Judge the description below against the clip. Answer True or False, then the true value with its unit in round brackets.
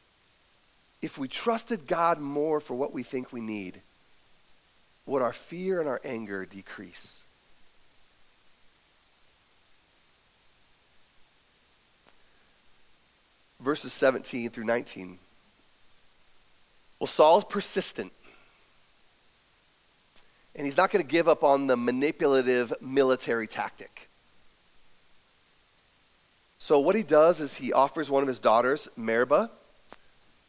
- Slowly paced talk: True (95 wpm)